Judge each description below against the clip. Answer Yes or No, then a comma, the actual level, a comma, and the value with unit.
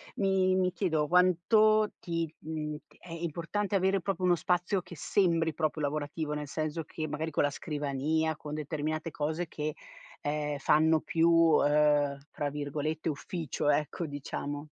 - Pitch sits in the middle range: Yes, medium, 155 Hz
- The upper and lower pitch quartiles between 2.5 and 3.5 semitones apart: Yes, average, 2.8 semitones